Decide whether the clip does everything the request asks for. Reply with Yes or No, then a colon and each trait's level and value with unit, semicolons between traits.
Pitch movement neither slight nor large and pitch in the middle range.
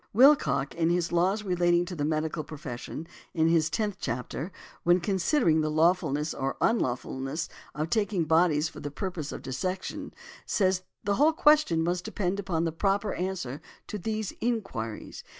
Yes: average, 4.1 semitones; medium, 170 Hz